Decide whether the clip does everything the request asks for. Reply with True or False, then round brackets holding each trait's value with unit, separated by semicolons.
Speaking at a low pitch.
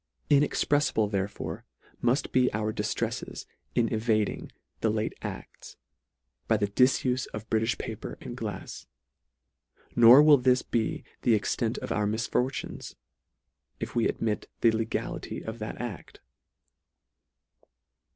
True (115 Hz)